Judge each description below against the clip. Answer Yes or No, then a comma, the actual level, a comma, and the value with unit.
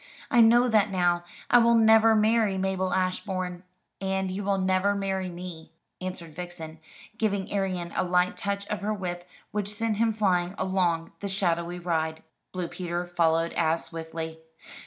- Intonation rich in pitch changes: No, narrow, 2.6 semitones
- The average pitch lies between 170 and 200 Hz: Yes, medium, 185 Hz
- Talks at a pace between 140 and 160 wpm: Yes, average, 155 wpm